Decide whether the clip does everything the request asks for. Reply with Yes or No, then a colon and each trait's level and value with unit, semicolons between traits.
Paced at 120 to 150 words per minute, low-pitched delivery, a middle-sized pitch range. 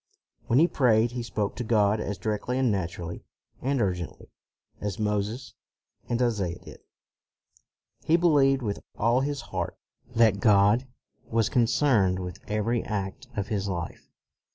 Yes: average, 140 wpm; low, 110 Hz; average, 3.7 semitones